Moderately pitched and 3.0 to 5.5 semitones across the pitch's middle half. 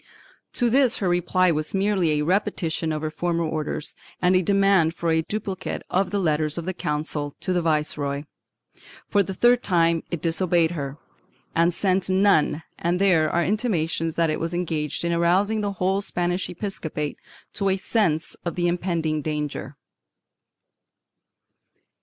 Yes: medium, 170 Hz; average, 3.3 semitones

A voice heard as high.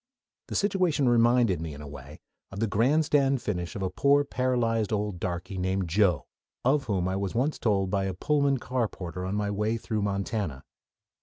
No: low, 105 Hz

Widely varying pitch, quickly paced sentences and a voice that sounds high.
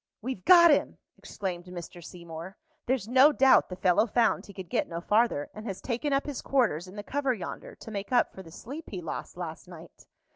Yes: wide, 6.5 semitones; fast, 215 wpm; high, 205 Hz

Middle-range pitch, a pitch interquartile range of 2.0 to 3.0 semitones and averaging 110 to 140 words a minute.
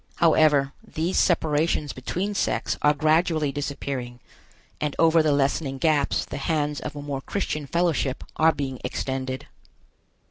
Yes: medium, 150 Hz; average, 2.7 semitones; slow, 135 wpm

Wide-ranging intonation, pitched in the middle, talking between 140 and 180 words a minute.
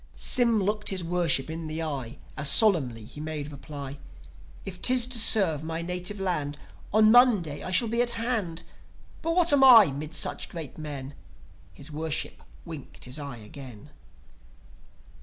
Yes: wide, 6.8 semitones; medium, 165 Hz; average, 160 wpm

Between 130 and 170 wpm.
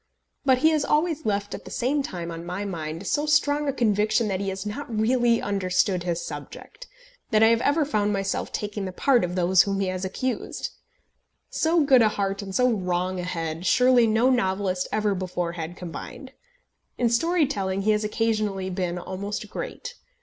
No: average, 190 wpm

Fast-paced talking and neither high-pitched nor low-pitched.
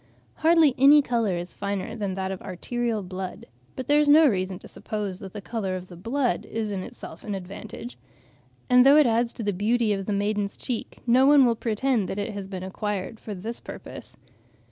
No: fast, 210 wpm; high, 210 Hz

